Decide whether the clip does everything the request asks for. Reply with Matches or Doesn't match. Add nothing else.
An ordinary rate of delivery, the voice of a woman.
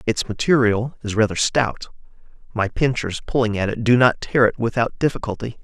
Doesn't match